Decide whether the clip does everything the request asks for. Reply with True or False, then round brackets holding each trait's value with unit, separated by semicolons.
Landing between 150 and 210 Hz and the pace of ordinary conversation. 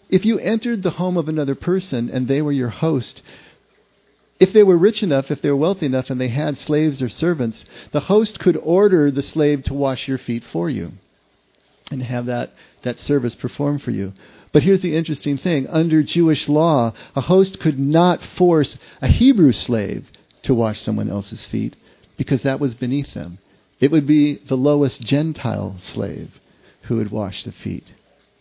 False (140 Hz; 185 wpm)